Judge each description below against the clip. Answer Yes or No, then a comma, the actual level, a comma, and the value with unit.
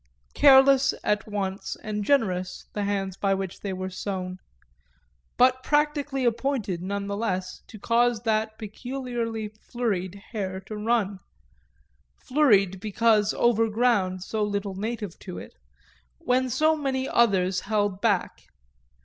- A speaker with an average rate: No, slow, 130 wpm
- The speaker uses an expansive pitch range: No, average, 3.8 semitones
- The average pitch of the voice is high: Yes, high, 215 Hz